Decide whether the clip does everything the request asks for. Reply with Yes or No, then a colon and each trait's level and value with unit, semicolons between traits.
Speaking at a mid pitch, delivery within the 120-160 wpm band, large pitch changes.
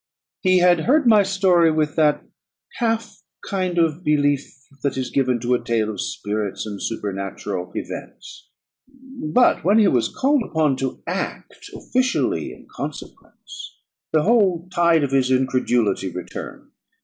Yes: medium, 155 Hz; average, 140 wpm; wide, 7.3 semitones